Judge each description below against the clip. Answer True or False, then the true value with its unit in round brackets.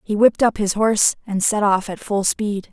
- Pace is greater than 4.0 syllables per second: True (5.2 syllables/s)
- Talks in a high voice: True (205 Hz)